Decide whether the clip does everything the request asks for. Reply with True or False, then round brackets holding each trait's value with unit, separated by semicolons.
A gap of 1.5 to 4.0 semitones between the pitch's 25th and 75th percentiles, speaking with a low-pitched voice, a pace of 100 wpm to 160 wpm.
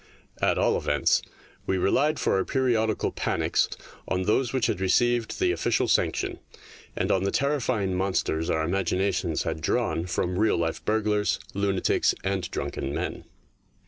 True (3.6 semitones; 95 Hz; 145 wpm)